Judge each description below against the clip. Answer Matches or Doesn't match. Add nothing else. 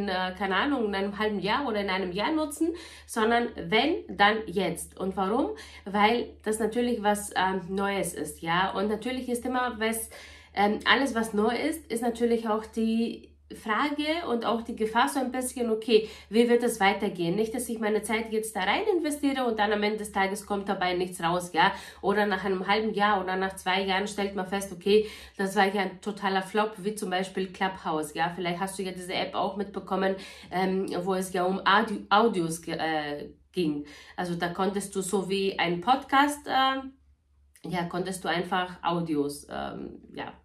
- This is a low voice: Doesn't match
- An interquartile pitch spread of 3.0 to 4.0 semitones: Matches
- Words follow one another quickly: Matches